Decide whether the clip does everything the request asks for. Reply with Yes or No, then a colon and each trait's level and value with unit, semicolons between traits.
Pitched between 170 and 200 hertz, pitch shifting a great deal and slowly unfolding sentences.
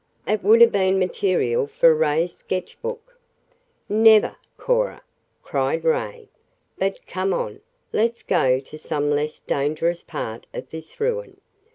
Yes: high, 190 Hz; wide, 7.2 semitones; slow, 130 wpm